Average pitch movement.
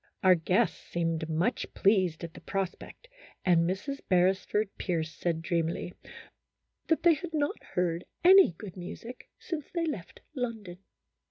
No: wide, 6.5 semitones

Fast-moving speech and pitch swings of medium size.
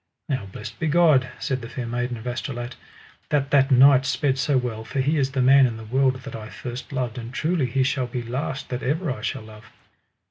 No: fast, 225 wpm; narrow, 2.3 semitones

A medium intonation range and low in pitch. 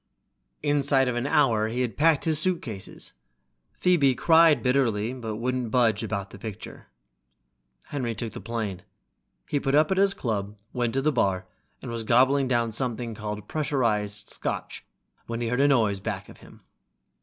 Yes: average, 4.2 semitones; low, 120 Hz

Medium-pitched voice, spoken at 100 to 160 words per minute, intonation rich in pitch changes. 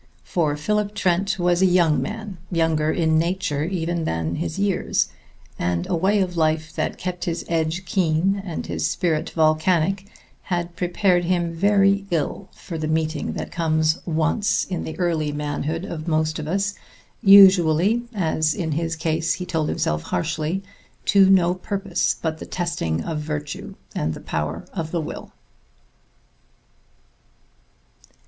No: medium, 170 Hz; average, 150 wpm; average, 3.1 semitones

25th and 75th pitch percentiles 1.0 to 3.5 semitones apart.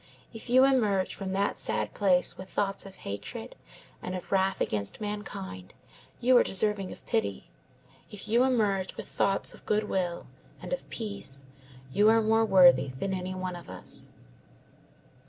Yes: average, 2.9 semitones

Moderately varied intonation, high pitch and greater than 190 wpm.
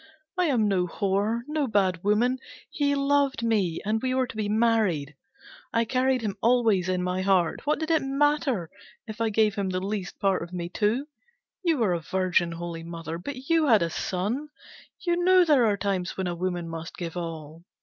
No: wide, 6.3 semitones; high, 210 Hz; average, 200 wpm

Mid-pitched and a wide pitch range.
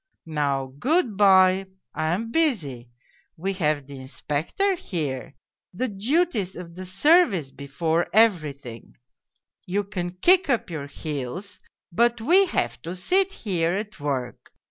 Yes: medium, 180 Hz; wide, 7.5 semitones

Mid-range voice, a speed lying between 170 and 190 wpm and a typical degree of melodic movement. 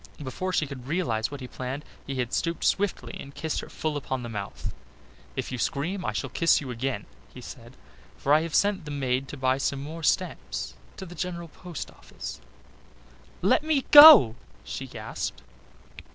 Yes: medium, 145 Hz; average, 180 wpm; average, 5.0 semitones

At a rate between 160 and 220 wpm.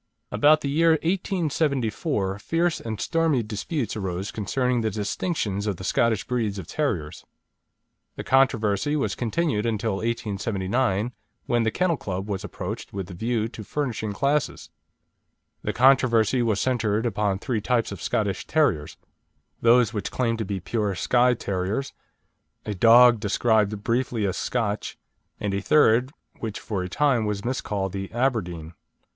No: average, 145 wpm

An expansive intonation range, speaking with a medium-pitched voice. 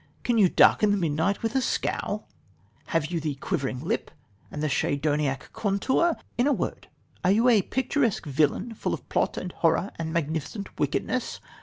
Yes: wide, 6.9 semitones; medium, 175 Hz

